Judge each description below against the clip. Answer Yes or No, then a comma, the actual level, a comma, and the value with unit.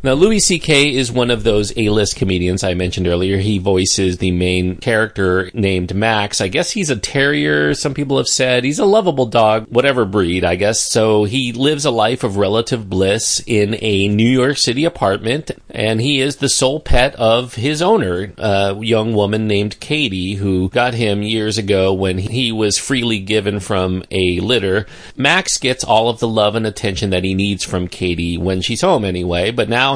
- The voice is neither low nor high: No, low, 105 Hz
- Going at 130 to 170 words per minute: No, average, 195 wpm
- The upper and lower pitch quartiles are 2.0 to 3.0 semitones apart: No, average, 4.8 semitones